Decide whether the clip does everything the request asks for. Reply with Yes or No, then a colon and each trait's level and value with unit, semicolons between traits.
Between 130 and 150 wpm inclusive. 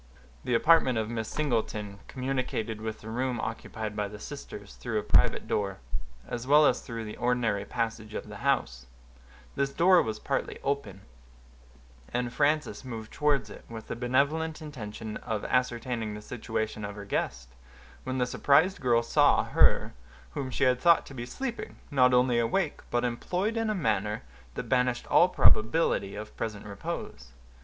No: average, 165 wpm